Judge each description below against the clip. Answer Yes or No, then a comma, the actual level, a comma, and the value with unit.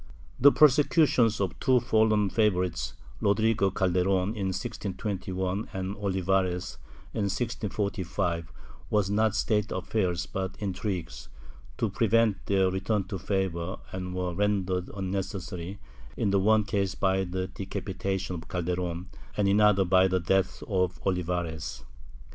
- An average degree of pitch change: No, narrow, 2.1 semitones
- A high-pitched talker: No, very low, 95 Hz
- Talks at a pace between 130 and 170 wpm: Yes, slow, 135 wpm